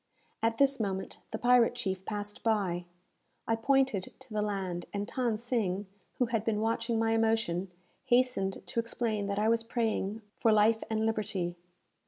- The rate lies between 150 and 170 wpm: Yes, average, 165 wpm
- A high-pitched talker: Yes, high, 220 Hz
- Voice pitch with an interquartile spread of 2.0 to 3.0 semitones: Yes, narrow, 2.4 semitones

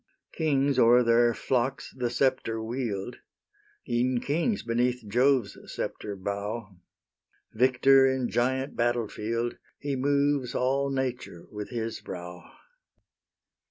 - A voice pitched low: Yes, low, 125 Hz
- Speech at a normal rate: No, slow, 110 wpm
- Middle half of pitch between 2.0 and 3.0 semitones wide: Yes, average, 2.7 semitones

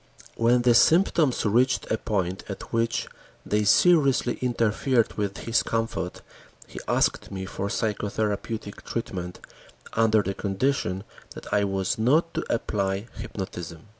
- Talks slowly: Yes, slow, 130 wpm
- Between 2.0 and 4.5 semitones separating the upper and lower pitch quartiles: Yes, average, 3.6 semitones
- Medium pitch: No, low, 110 Hz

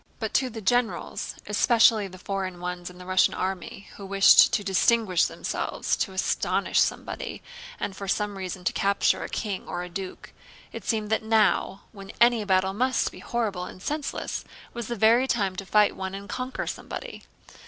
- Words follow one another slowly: No, average, 165 wpm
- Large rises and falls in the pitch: No, average, 3.2 semitones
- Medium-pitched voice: No, high, 200 Hz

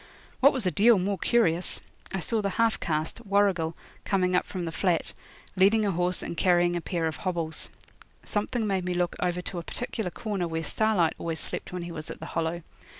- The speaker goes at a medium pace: No, fast, 210 wpm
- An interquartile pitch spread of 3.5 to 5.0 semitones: No, average, 3.1 semitones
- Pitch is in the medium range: Yes, medium, 180 Hz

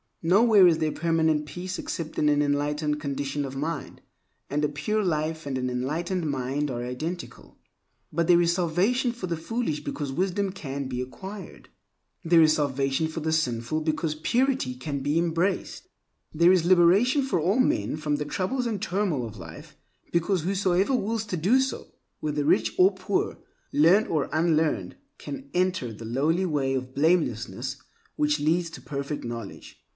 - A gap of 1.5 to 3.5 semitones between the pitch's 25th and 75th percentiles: No, average, 4.5 semitones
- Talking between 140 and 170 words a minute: Yes, average, 160 wpm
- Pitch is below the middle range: No, medium, 160 Hz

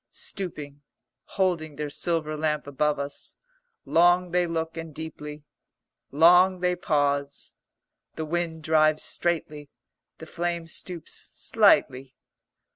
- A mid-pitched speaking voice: Yes, medium, 160 Hz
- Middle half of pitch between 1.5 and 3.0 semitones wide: Yes, narrow, 2.5 semitones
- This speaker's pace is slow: Yes, slow, 110 wpm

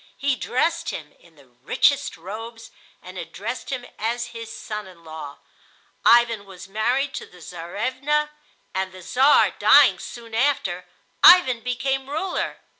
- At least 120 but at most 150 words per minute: Yes, average, 140 wpm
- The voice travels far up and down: Yes, wide, 6.3 semitones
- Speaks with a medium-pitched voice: No, high, 230 Hz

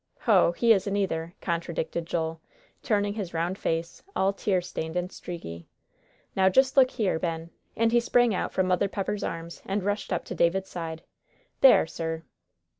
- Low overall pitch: No, medium, 180 Hz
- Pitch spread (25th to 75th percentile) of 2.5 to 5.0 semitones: Yes, average, 3.5 semitones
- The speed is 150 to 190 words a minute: Yes, average, 170 wpm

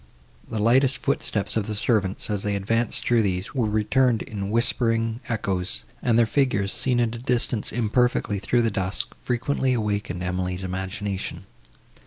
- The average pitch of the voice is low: Yes, low, 110 Hz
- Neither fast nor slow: Yes, average, 155 wpm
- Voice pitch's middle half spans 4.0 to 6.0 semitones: No, average, 3.3 semitones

